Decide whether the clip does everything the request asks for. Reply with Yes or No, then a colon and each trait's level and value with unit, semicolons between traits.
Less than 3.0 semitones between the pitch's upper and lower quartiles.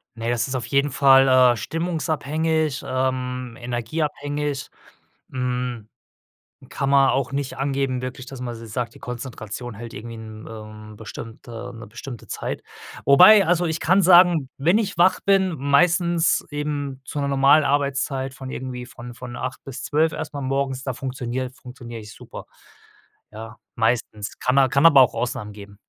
No: average, 3.3 semitones